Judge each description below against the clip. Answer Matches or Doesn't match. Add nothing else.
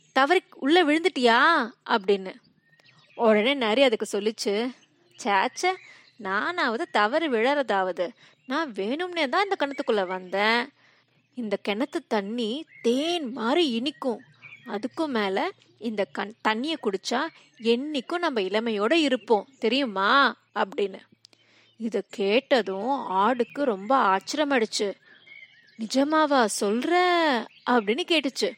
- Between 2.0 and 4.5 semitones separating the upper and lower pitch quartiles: Doesn't match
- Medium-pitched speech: Doesn't match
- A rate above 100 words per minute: Doesn't match